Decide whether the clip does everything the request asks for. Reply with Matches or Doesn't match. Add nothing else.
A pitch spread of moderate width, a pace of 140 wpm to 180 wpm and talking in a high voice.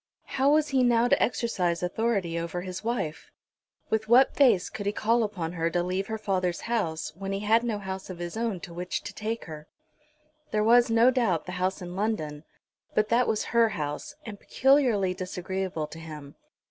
Doesn't match